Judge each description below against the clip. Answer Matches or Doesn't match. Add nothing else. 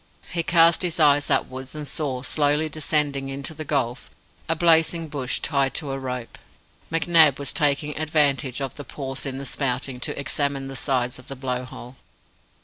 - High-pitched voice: Doesn't match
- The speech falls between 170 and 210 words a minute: Matches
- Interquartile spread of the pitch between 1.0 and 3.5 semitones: Matches